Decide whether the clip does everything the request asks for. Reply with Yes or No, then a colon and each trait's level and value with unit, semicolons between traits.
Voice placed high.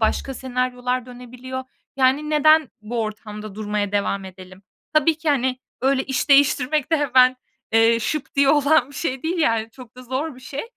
Yes: very high, 255 Hz